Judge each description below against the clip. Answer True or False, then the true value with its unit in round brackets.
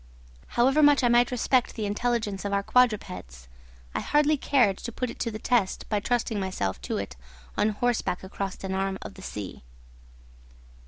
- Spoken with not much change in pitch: False (4.1 semitones)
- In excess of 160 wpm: True (175 wpm)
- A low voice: False (215 Hz)